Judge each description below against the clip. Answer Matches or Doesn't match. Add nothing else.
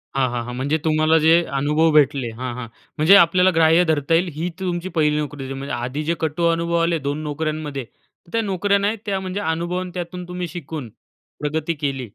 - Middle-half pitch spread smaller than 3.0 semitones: Doesn't match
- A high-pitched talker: Doesn't match